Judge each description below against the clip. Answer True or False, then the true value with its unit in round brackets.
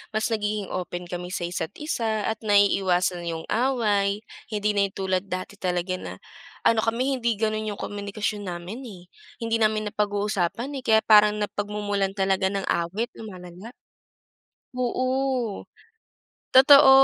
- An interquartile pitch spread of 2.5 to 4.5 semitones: True (2.9 semitones)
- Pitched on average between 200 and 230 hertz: True (205 Hz)